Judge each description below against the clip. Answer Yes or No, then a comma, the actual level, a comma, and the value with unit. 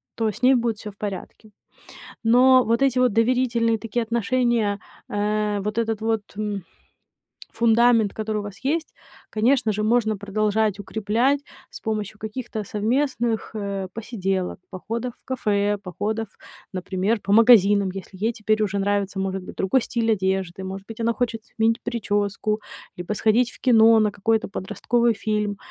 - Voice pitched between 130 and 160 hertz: No, high, 215 Hz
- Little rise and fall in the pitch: Yes, narrow, 2.3 semitones